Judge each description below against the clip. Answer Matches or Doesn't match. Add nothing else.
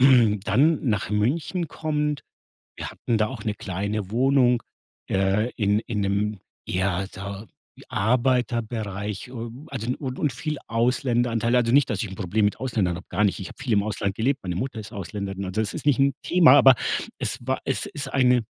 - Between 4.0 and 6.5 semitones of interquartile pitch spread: Matches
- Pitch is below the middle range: Matches